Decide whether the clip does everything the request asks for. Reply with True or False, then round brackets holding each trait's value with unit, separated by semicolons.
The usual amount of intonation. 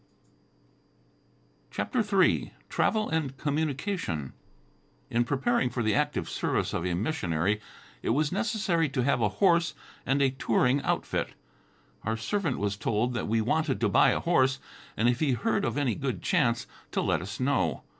False (6.4 semitones)